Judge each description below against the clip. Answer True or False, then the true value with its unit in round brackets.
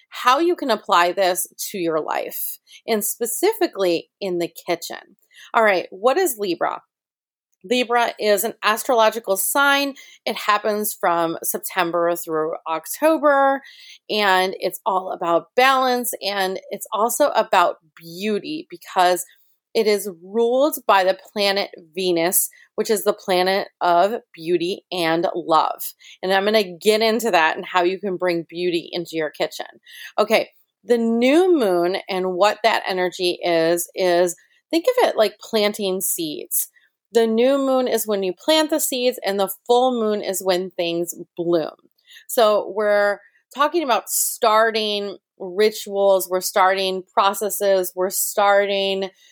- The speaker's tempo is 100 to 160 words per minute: True (140 wpm)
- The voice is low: False (200 Hz)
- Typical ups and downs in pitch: True (4.7 semitones)